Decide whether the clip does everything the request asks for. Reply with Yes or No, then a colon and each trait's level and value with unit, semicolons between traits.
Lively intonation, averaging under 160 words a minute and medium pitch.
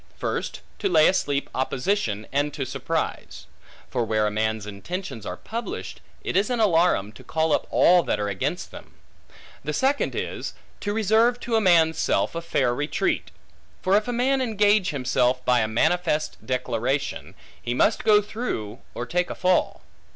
No: wide, 9.0 semitones; average, 170 wpm; medium, 160 Hz